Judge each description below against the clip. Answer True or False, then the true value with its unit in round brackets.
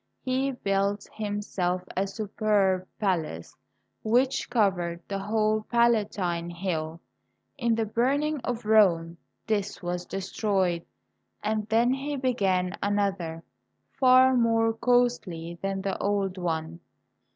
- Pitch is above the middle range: True (205 Hz)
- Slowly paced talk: True (115 wpm)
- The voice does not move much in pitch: False (4.2 semitones)